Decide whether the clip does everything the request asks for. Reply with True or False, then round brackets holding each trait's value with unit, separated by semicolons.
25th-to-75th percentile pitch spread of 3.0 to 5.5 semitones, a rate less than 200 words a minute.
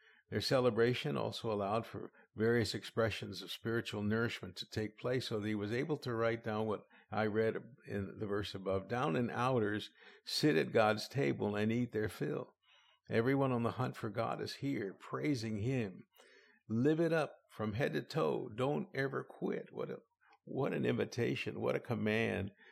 False (2.4 semitones; 175 wpm)